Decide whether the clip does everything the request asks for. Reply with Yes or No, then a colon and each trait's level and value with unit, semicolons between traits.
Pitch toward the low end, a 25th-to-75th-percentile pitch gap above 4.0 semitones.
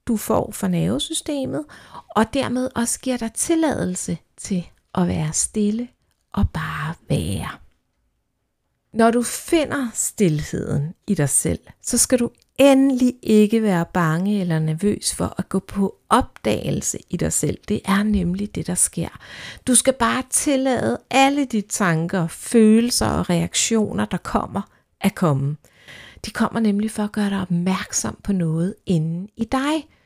No: high, 210 Hz; average, 5.1 semitones